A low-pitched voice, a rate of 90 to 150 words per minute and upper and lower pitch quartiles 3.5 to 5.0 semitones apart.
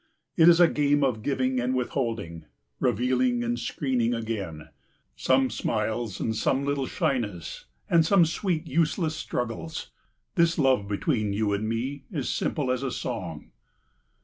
Yes: low, 125 Hz; average, 145 wpm; average, 4.4 semitones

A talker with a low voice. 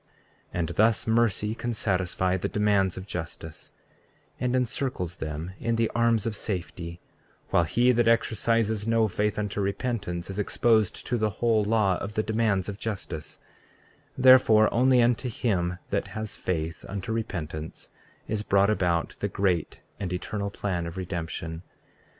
Yes: low, 105 Hz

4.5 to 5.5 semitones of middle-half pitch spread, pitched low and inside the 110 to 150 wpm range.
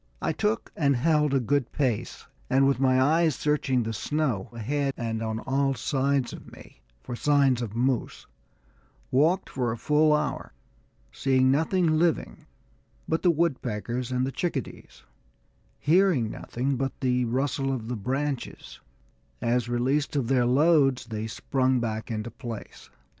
No: average, 3.4 semitones; low, 130 Hz; average, 145 wpm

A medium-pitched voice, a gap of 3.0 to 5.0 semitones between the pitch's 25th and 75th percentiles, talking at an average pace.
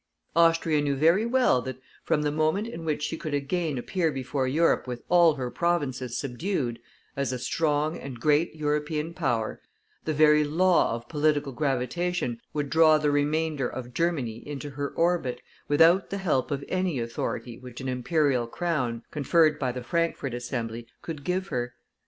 Yes: medium, 150 Hz; average, 4.4 semitones; average, 165 wpm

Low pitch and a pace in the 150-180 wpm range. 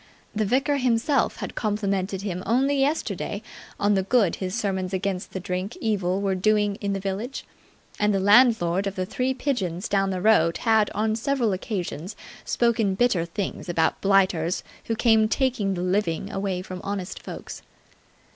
No: high, 200 Hz; average, 165 wpm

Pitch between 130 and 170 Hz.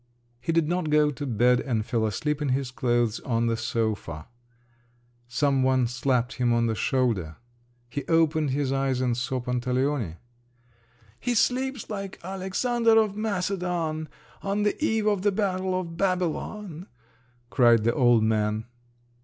Yes: medium, 140 Hz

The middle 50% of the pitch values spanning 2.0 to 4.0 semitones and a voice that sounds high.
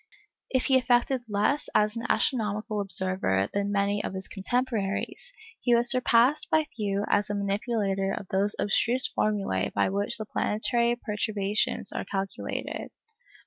Yes: average, 3.3 semitones; high, 210 Hz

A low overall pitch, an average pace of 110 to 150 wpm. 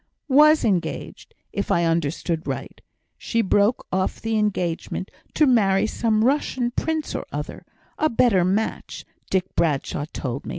No: high, 205 Hz; average, 140 wpm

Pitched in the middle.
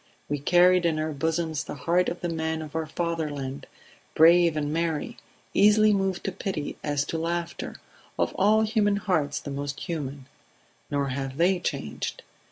Yes: medium, 160 Hz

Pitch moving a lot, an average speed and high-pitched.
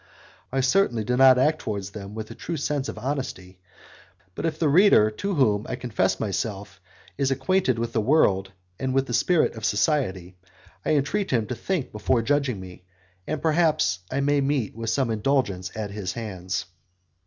No: wide, 5.7 semitones; average, 180 wpm; low, 125 Hz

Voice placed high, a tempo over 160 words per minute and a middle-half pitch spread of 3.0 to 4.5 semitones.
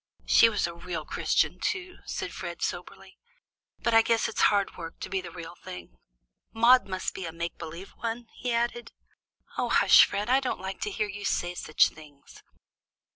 No: high, 195 Hz; average, 185 wpm; average, 5.3 semitones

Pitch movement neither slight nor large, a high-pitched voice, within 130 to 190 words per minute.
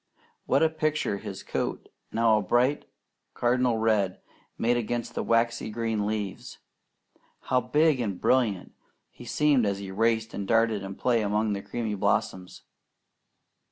No: average, 3.0 semitones; low, 115 Hz; average, 145 wpm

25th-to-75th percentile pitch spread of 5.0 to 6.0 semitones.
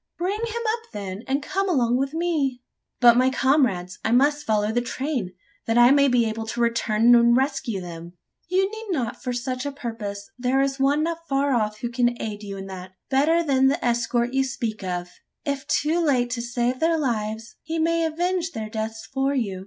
No: average, 4.4 semitones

